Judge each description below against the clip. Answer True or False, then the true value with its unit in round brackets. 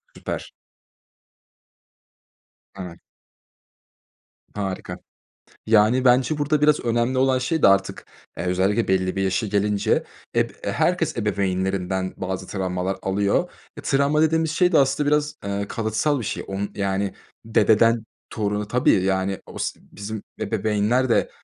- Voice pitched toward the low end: True (105 Hz)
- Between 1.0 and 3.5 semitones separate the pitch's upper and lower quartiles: False (5.1 semitones)